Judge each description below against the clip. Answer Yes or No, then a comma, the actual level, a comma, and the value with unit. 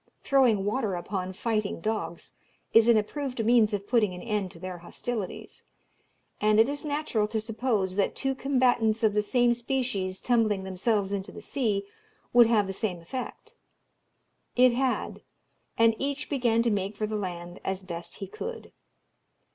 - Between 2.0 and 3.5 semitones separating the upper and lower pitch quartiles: No, average, 4.1 semitones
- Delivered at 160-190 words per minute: Yes, average, 165 wpm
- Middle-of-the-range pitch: No, high, 215 Hz